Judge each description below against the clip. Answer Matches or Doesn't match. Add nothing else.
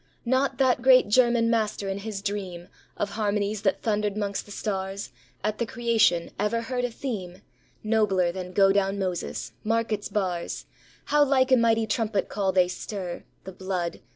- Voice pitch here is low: Doesn't match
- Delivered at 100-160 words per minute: Doesn't match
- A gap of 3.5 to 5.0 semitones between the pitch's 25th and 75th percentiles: Doesn't match